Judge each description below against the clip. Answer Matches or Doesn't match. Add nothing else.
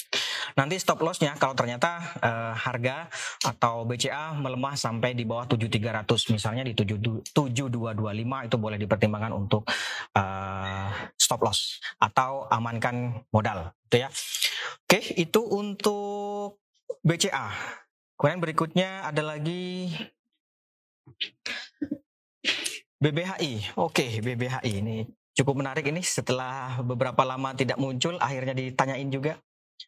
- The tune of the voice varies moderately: Doesn't match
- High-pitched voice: Doesn't match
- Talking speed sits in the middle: Matches